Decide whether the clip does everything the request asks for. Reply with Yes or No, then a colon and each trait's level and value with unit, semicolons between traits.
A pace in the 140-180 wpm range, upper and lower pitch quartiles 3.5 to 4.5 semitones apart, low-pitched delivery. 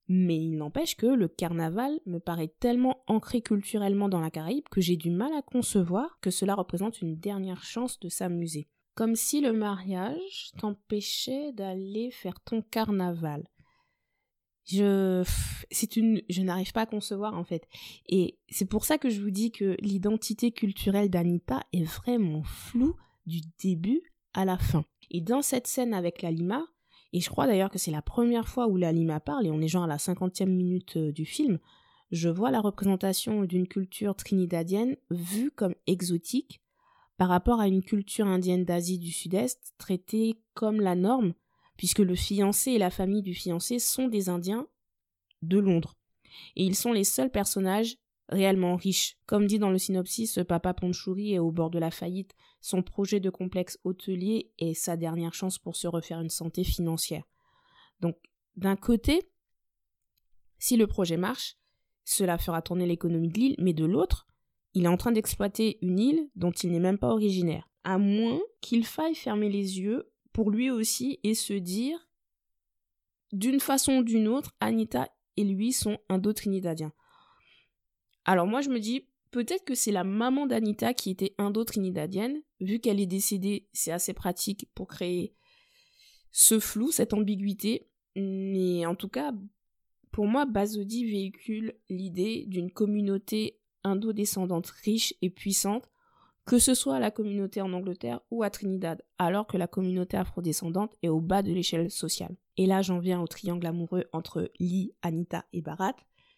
No: average, 170 wpm; average, 4.0 semitones; high, 195 Hz